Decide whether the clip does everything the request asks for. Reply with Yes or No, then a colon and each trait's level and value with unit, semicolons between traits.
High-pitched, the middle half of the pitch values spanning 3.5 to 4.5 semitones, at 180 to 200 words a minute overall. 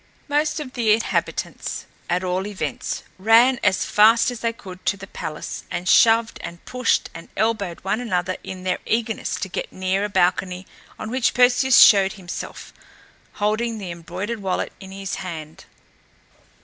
No: high, 200 Hz; average, 3.8 semitones; average, 160 wpm